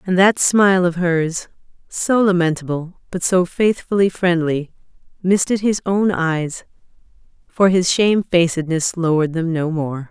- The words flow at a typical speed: No, slow, 130 wpm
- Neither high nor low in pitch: Yes, medium, 175 Hz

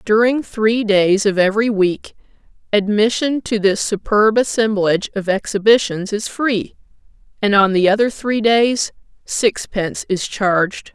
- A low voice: No, high, 210 Hz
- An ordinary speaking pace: No, slow, 130 wpm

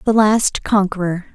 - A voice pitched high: Yes, high, 200 Hz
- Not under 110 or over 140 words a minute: Yes, slow, 135 wpm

